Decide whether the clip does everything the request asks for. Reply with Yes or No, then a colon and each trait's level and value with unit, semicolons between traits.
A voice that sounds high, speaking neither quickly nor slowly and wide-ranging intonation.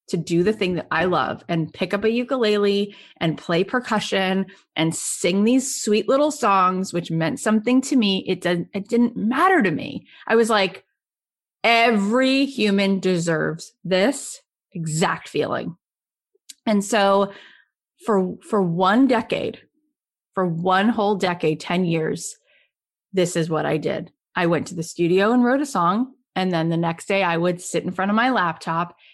No: high, 195 Hz; average, 165 wpm; average, 4.6 semitones